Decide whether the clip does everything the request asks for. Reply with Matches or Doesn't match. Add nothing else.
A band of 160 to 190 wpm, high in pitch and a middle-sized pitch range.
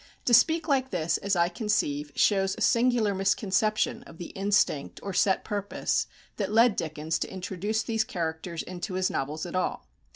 Matches